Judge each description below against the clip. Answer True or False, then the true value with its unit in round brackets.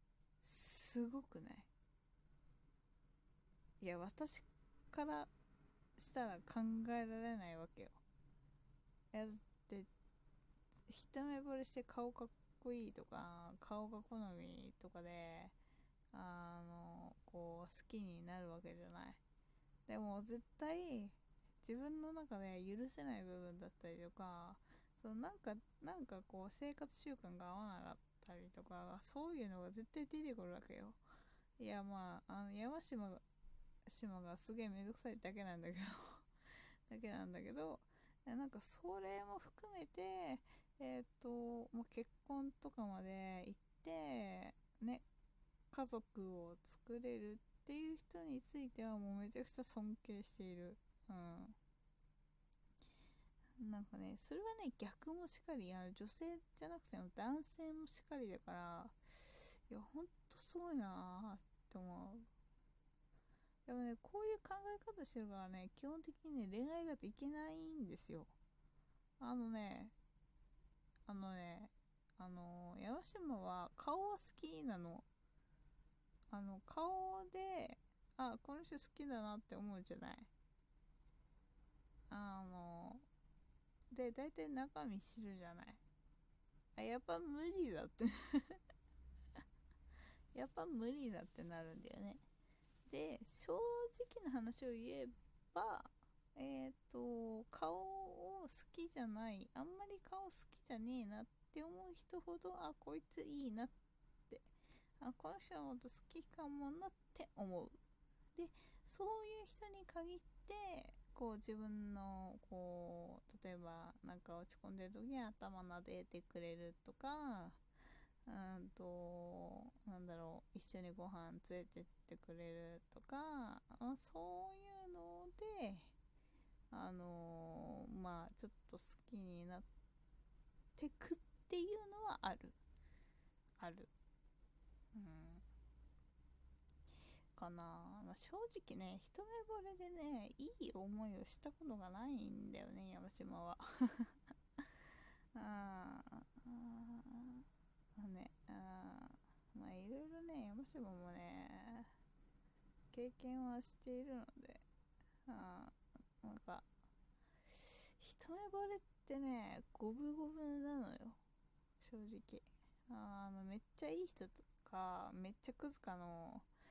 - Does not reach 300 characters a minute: True (225 characters per minute)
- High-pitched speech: True (225 Hz)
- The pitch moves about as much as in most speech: False (7.4 semitones)